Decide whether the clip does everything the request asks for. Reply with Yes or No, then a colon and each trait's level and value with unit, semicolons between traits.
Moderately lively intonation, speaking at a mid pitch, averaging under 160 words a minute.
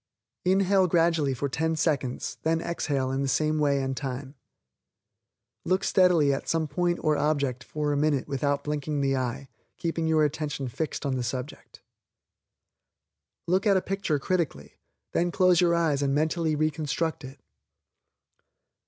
Yes: average, 3.3 semitones; medium, 150 Hz; average, 150 wpm